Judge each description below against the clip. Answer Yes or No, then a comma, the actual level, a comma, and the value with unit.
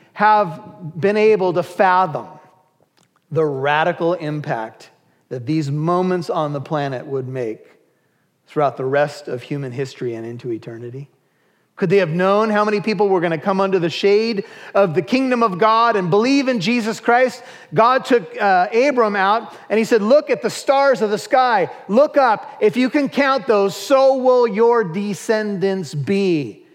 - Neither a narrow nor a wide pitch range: No, wide, 6.7 semitones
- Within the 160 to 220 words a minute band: Yes, average, 170 wpm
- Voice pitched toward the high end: Yes, high, 200 Hz